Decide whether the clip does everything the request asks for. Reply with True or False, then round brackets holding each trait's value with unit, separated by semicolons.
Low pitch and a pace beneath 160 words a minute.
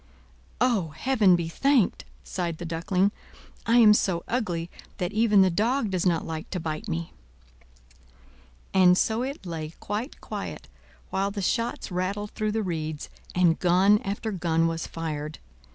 False (185 Hz; 150 wpm)